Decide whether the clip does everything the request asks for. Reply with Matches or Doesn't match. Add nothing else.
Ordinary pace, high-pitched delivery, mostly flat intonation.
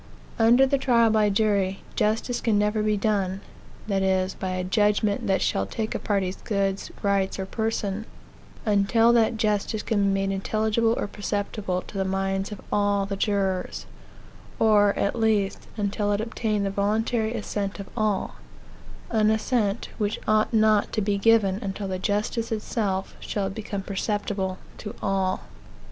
Matches